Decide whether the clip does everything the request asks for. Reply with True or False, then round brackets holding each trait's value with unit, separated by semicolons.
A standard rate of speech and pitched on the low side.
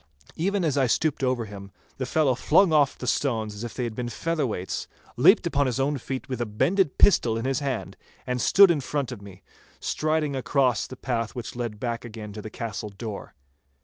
False (210 wpm; 125 Hz)